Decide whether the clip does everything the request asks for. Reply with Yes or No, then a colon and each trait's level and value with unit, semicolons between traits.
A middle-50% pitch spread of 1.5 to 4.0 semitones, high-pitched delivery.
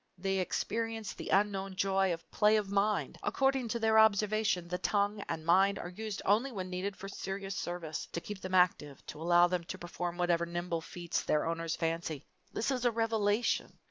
Yes: average, 3.4 semitones; high, 195 Hz